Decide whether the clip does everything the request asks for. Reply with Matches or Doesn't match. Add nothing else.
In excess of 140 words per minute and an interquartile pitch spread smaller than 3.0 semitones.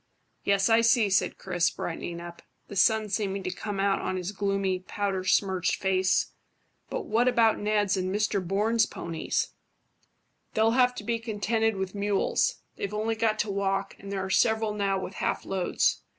Matches